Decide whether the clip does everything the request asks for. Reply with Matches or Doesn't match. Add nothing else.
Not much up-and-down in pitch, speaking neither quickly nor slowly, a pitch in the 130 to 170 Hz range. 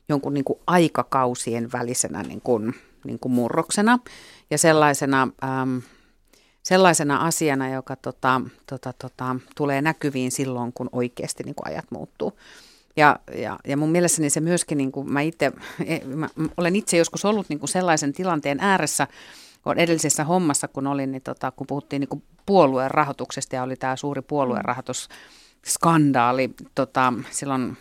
Doesn't match